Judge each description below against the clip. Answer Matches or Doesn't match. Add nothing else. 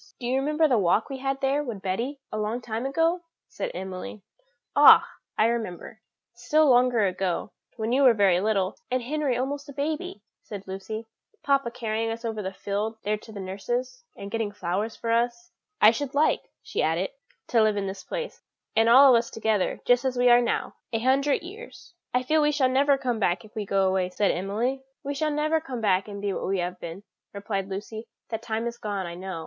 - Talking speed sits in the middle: Doesn't match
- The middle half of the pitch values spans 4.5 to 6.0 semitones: Matches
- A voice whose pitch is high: Matches